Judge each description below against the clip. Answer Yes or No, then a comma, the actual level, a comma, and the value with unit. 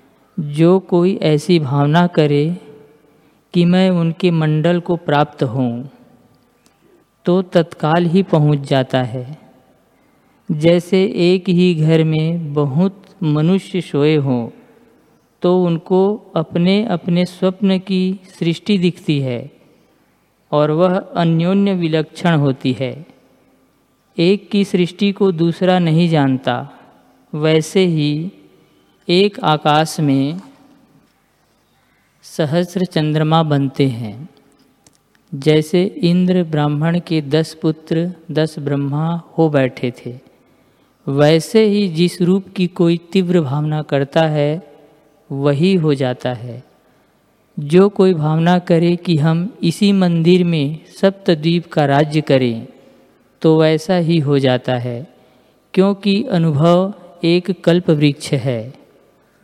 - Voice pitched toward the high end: No, medium, 165 Hz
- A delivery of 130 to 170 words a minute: No, slow, 110 wpm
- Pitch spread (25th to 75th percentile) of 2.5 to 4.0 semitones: Yes, average, 3.6 semitones